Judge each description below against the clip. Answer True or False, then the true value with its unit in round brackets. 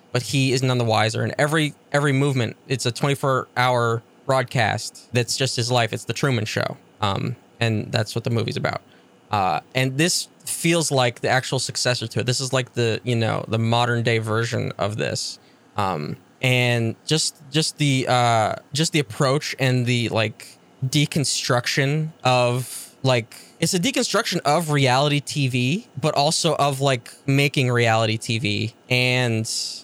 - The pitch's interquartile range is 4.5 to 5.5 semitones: False (3.3 semitones)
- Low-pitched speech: True (125 Hz)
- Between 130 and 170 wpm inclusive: True (155 wpm)